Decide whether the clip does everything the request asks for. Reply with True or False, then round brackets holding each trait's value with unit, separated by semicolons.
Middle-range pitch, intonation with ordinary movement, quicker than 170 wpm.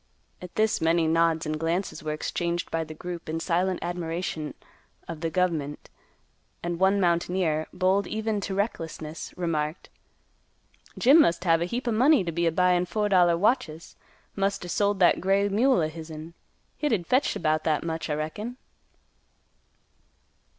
False (175 Hz; 3.4 semitones; 155 wpm)